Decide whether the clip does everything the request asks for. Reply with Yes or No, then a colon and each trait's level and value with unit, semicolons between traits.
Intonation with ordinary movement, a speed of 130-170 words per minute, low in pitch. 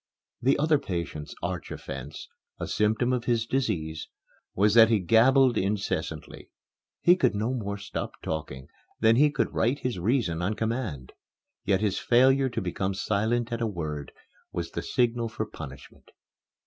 Yes: average, 4.8 semitones; average, 155 wpm; low, 110 Hz